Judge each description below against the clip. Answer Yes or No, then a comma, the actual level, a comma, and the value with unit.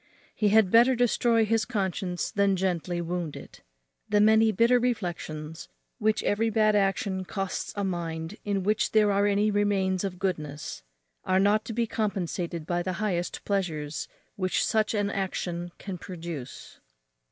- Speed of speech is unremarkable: Yes, average, 150 wpm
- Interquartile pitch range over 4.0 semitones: No, average, 3.4 semitones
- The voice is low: No, high, 195 Hz